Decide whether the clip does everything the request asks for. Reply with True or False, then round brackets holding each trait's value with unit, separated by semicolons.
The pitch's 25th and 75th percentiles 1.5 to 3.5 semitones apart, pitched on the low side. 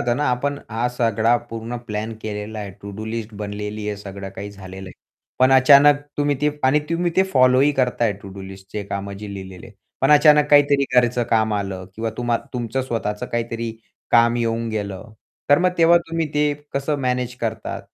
False (4.4 semitones; 115 Hz)